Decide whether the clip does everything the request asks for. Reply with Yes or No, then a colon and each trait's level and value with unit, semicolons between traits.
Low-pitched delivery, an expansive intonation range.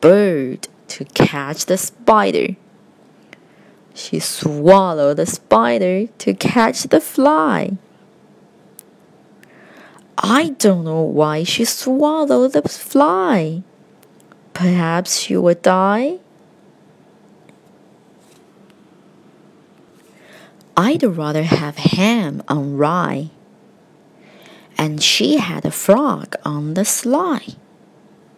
No: high, 195 Hz; wide, 6.1 semitones